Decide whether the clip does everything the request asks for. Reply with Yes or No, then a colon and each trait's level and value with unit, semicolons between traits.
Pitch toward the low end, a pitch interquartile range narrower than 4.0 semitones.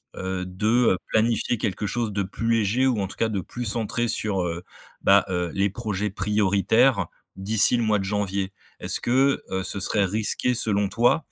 Yes: low, 105 Hz; average, 3.0 semitones